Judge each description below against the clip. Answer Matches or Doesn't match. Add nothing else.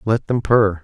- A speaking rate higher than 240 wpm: Doesn't match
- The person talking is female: Doesn't match